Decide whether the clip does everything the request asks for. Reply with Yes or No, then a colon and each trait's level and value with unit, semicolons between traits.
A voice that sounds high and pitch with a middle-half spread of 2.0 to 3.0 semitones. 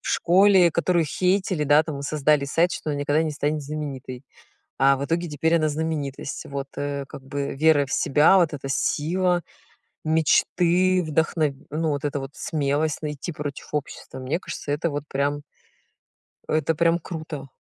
No: medium, 150 Hz; average, 2.7 semitones